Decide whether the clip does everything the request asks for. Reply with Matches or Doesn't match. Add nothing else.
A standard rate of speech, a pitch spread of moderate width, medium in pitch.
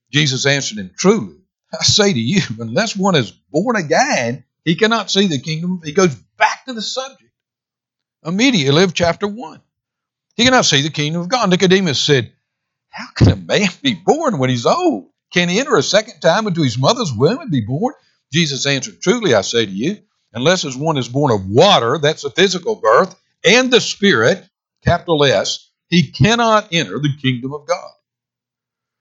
Doesn't match